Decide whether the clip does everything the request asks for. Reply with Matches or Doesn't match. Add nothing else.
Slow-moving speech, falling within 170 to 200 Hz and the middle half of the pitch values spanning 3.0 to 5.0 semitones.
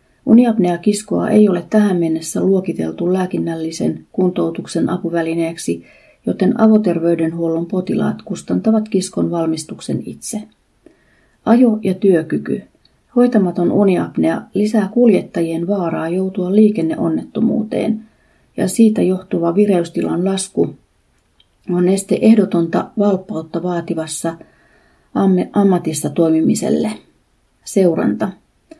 Matches